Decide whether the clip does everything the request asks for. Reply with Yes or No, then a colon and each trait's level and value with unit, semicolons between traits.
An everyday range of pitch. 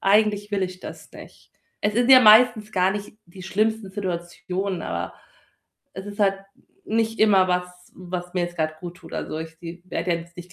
Yes: average, 3.1 semitones